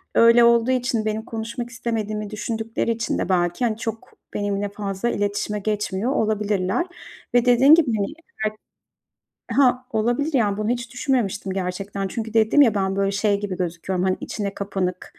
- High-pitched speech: Yes, high, 215 Hz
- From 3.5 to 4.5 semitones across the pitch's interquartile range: No, average, 3.0 semitones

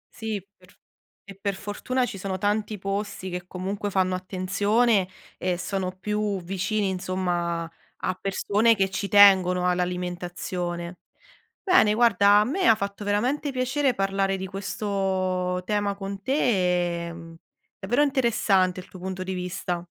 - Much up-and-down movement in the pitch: No, narrow, 2.4 semitones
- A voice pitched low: No, high, 195 Hz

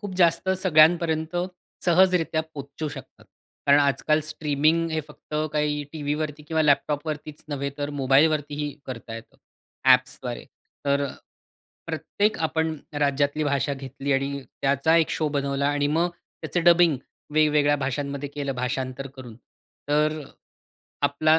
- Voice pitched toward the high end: No, medium, 145 Hz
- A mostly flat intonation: Yes, narrow, 2.2 semitones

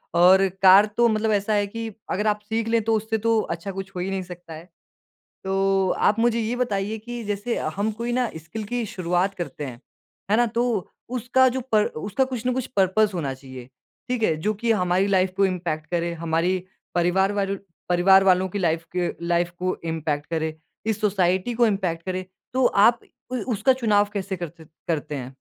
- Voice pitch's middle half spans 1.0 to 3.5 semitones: No, average, 4.0 semitones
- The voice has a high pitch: Yes, high, 195 Hz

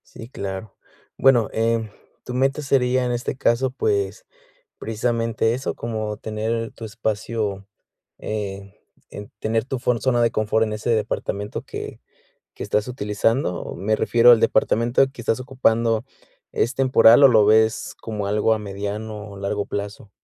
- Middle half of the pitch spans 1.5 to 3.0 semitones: Yes, narrow, 2.5 semitones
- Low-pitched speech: Yes, low, 115 Hz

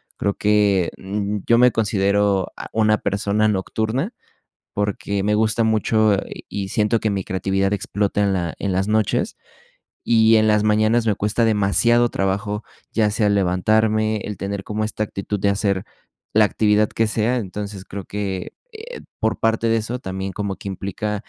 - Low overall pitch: Yes, low, 105 Hz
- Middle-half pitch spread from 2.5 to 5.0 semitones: No, narrow, 1.7 semitones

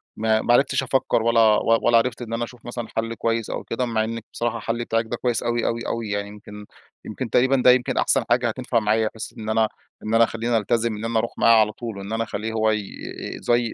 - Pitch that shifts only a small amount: Yes, narrow, 1.3 semitones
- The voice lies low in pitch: Yes, low, 115 Hz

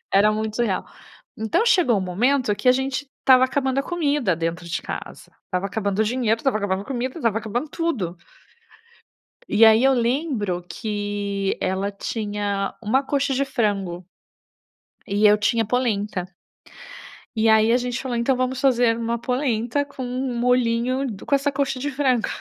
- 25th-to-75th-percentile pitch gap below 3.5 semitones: No, average, 4.2 semitones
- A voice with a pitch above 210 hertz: Yes, high, 235 Hz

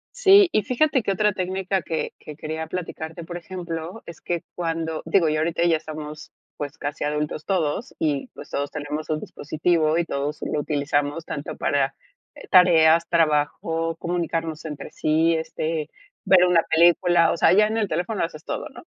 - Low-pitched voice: No, medium, 165 Hz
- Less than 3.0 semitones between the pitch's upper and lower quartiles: Yes, narrow, 2.5 semitones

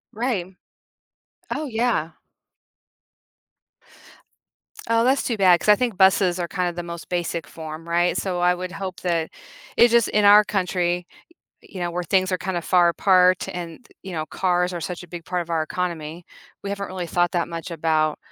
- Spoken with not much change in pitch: Yes, narrow, 2.0 semitones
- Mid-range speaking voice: Yes, medium, 180 Hz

